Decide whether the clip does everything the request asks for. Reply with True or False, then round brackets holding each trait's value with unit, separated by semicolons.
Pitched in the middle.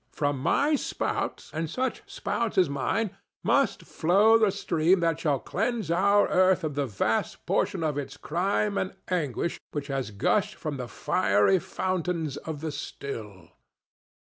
True (165 Hz)